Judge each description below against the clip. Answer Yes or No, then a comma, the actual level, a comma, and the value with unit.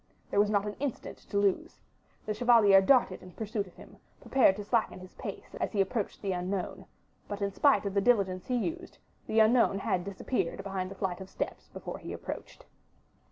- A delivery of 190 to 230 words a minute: Yes, average, 200 wpm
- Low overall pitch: No, high, 200 Hz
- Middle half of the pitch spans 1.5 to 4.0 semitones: Yes, average, 2.8 semitones